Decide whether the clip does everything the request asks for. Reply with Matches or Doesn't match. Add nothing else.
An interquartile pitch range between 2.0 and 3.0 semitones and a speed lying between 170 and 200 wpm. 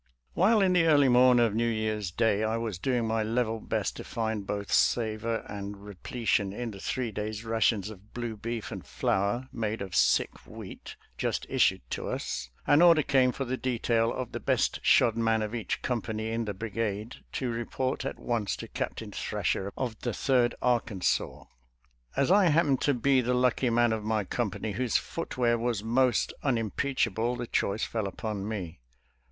Matches